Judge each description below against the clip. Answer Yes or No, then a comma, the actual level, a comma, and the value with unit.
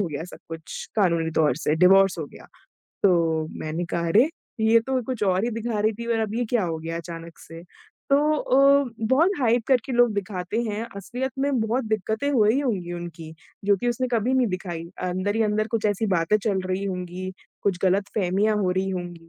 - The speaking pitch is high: Yes, high, 200 Hz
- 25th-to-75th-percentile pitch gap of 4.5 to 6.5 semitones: Yes, average, 4.8 semitones